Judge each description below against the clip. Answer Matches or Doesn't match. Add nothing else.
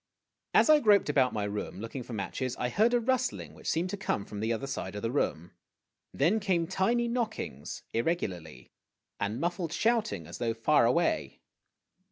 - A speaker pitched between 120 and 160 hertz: Matches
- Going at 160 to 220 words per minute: Matches